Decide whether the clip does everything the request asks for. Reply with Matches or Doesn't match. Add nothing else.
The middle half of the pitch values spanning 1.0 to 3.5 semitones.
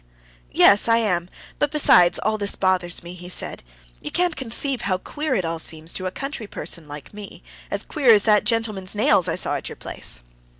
Doesn't match